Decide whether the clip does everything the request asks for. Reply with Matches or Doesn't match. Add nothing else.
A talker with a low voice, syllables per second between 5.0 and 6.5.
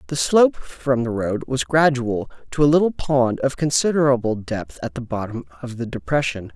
Matches